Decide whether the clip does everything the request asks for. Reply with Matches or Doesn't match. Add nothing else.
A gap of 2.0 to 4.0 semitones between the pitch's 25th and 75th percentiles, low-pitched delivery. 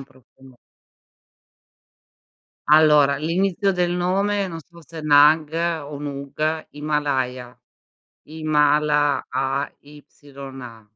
Doesn't match